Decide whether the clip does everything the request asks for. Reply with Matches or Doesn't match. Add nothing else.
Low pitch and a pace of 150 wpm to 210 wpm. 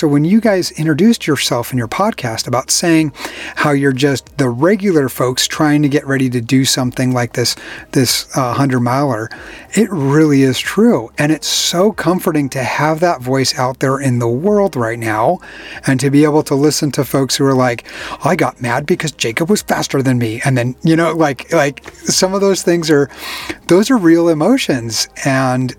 Doesn't match